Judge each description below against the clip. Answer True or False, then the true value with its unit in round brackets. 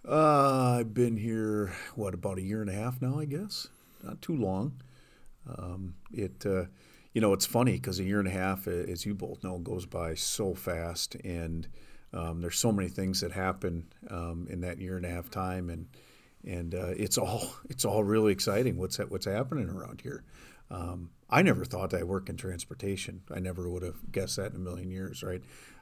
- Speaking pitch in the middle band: False (95 Hz)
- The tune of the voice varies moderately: True (3.1 semitones)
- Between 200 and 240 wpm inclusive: True (205 wpm)